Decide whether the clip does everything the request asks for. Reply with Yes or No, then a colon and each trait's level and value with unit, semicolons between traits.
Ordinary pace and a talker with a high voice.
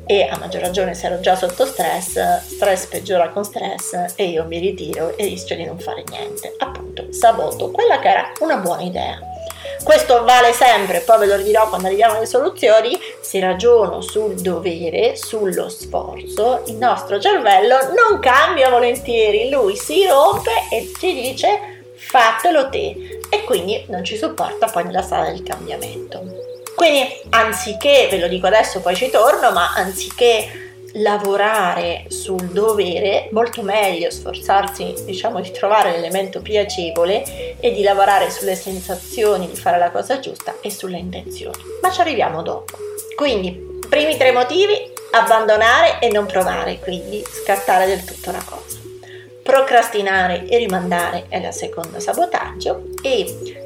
Yes: average, 150 wpm; high, 230 Hz